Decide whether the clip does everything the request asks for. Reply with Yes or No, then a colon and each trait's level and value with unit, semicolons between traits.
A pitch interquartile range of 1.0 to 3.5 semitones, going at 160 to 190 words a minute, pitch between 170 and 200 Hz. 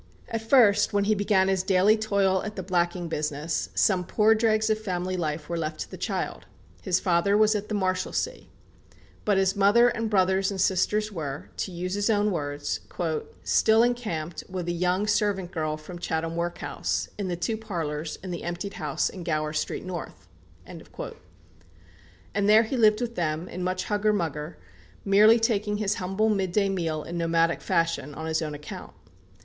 No: average, 3.9 semitones; average, 175 wpm; medium, 185 Hz